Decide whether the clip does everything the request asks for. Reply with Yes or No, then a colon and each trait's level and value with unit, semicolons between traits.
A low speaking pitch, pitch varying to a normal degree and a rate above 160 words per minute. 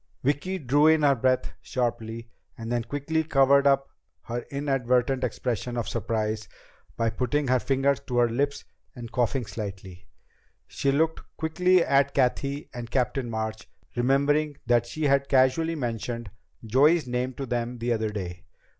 No: low, 130 Hz; average, 3.2 semitones; average, 145 wpm